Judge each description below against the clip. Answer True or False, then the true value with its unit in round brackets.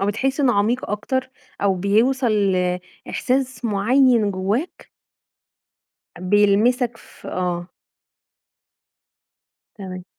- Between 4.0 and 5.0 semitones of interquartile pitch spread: True (4.6 semitones)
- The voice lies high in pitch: True (210 Hz)